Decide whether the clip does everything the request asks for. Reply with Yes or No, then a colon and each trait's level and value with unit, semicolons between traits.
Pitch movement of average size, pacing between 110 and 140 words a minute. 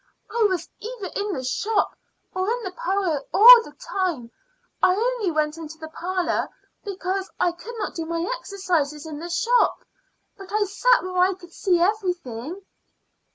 No: average, 3.8 semitones; average, 165 wpm